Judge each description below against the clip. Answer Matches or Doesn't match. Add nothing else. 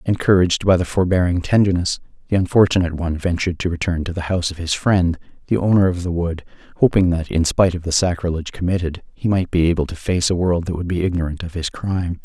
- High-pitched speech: Doesn't match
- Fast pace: Matches